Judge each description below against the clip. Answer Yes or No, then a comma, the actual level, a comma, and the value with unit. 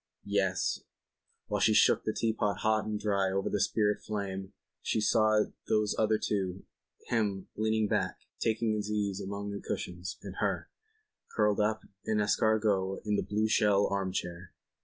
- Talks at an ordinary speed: Yes, average, 160 wpm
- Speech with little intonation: Yes, narrow, 1.7 semitones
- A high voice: No, low, 105 Hz